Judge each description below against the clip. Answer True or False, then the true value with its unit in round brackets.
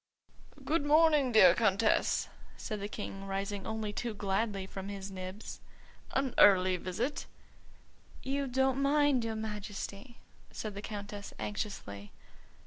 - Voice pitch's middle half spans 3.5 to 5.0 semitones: True (4.3 semitones)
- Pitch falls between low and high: False (210 Hz)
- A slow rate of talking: True (125 wpm)